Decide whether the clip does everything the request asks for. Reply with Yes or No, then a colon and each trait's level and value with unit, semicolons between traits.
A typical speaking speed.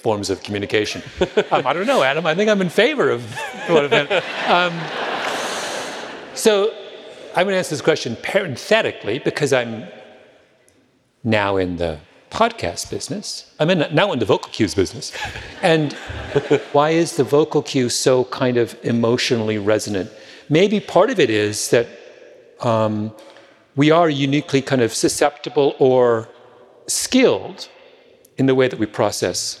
Yes: average, 145 wpm